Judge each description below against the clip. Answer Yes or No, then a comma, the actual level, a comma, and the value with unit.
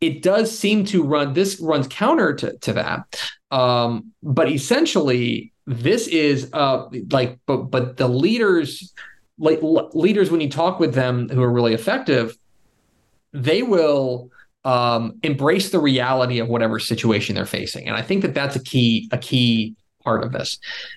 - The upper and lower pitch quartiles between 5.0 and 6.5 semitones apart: Yes, average, 5.3 semitones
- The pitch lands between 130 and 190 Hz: Yes, low, 135 Hz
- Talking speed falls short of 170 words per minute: Yes, average, 160 wpm